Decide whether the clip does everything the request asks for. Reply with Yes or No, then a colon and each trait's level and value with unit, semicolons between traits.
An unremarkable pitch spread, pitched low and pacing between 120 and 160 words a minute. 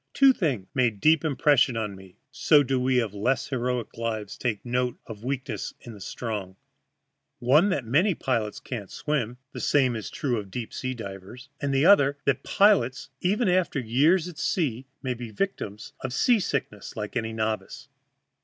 No: average, 4.6 semitones; low, 125 Hz; average, 170 wpm